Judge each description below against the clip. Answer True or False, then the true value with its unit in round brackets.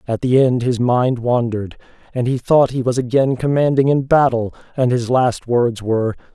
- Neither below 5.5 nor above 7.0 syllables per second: False (5.0 syllables/s)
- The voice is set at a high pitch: False (125 Hz)